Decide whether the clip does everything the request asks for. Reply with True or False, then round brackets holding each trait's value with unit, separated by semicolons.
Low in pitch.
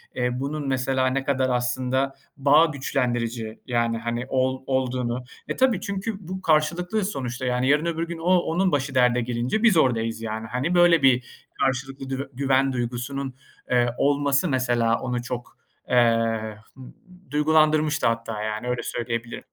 True (130 Hz)